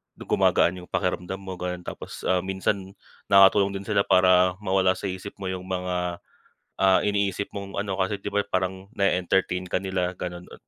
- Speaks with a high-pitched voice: No, very low, 95 Hz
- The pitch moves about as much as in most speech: No, narrow, 1.3 semitones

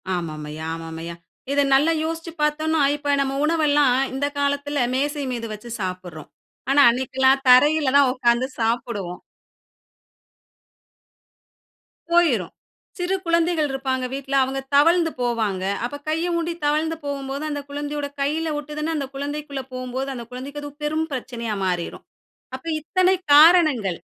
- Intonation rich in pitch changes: No, average, 3.8 semitones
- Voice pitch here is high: Yes, very high, 280 Hz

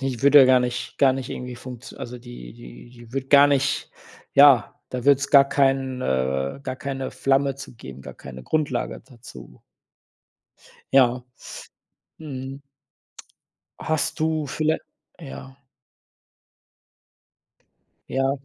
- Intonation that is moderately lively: No, narrow, 2.3 semitones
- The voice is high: No, low, 130 Hz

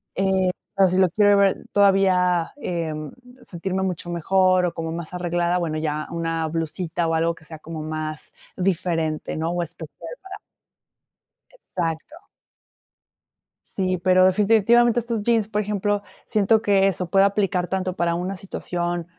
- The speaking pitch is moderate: Yes, medium, 180 Hz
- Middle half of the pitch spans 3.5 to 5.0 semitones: No, average, 2.9 semitones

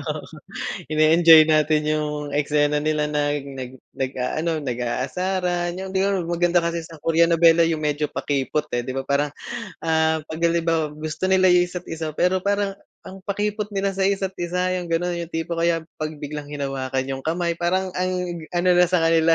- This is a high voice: No, medium, 165 Hz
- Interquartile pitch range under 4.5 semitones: Yes, average, 3.0 semitones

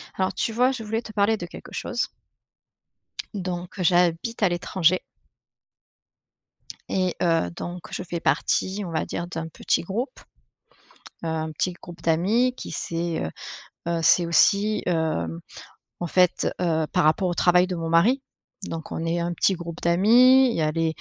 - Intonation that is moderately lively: Yes, average, 3.3 semitones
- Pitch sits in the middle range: Yes, medium, 175 Hz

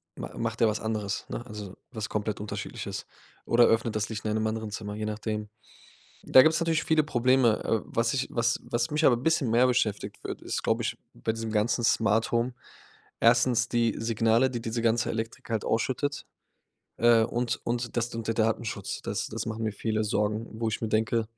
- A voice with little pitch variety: Yes, narrow, 1.6 semitones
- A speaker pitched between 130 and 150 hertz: No, low, 115 Hz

